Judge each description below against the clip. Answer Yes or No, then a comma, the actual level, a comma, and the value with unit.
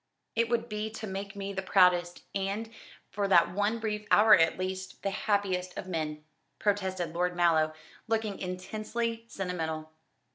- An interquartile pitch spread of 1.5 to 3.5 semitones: Yes, average, 2.9 semitones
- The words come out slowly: No, average, 150 wpm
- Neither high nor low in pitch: No, high, 195 Hz